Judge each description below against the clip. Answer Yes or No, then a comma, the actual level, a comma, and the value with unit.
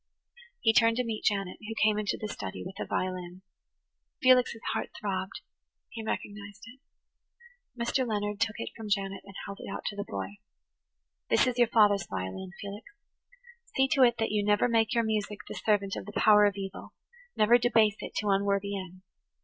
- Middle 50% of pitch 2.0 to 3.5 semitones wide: Yes, narrow, 2.4 semitones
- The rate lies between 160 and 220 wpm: Yes, average, 180 wpm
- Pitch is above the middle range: Yes, high, 210 Hz